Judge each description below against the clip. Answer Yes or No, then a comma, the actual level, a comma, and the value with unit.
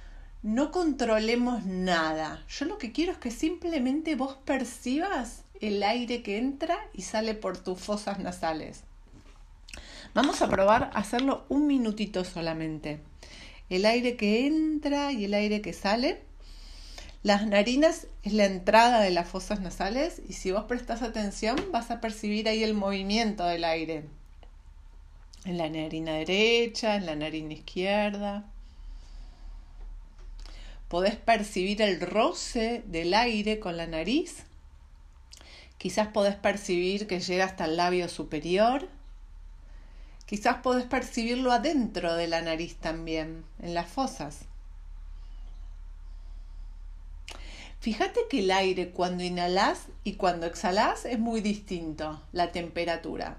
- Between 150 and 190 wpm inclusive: No, slow, 125 wpm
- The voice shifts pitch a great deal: Yes, wide, 6.6 semitones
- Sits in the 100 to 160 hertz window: No, high, 190 Hz